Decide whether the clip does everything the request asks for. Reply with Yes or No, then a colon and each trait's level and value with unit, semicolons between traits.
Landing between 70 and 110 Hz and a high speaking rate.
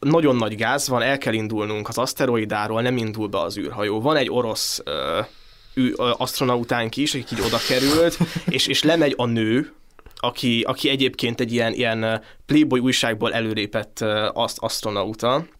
No: low, 120 Hz; fast, 160 wpm